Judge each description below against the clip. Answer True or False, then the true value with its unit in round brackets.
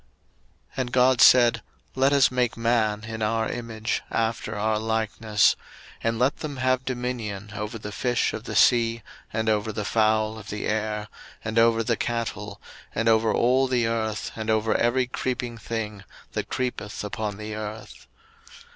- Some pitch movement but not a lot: False (2.1 semitones)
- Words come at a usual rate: True (165 wpm)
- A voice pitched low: True (115 Hz)